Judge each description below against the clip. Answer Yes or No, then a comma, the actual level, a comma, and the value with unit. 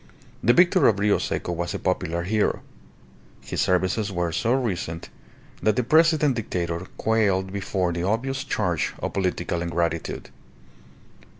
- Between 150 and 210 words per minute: No, slow, 135 wpm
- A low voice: Yes, very low, 95 Hz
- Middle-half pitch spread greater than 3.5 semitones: Yes, average, 4.7 semitones